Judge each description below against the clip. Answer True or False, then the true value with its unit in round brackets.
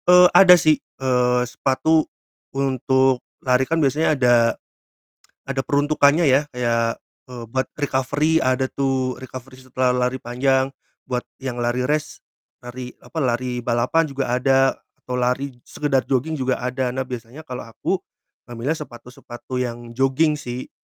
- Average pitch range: False (2.0 semitones)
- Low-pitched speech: True (130 Hz)